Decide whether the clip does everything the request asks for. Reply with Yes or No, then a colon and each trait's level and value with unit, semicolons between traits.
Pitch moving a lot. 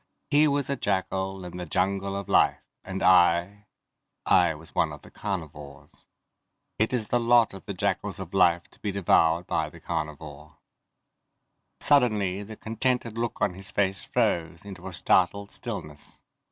No: average, 3.5 semitones